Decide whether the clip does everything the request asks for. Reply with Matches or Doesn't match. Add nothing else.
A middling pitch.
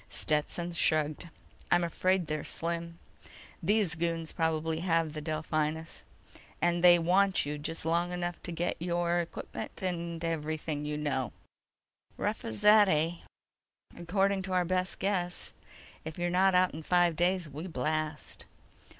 Matches